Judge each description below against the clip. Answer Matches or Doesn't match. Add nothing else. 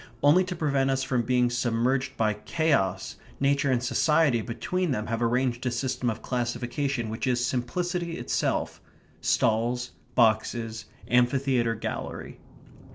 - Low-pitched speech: Matches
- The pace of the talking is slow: Matches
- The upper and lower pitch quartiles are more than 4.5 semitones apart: Doesn't match